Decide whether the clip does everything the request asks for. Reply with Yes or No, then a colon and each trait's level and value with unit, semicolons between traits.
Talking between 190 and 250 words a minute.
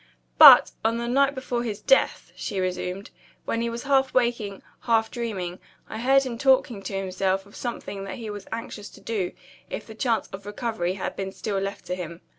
Yes: average, 200 wpm